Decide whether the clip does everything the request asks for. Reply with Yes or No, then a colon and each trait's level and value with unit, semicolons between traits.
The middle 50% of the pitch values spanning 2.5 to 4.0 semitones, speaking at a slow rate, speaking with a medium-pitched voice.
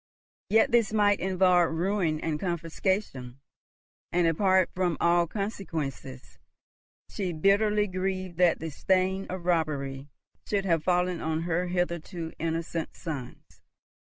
Yes: average, 2.8 semitones; slow, 120 wpm; medium, 175 Hz